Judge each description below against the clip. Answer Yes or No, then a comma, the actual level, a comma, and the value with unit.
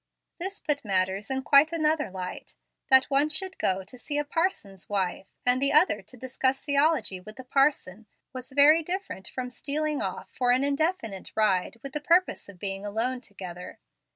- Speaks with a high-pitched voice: Yes, very high, 260 Hz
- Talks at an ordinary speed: Yes, average, 180 wpm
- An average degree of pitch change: No, wide, 6.9 semitones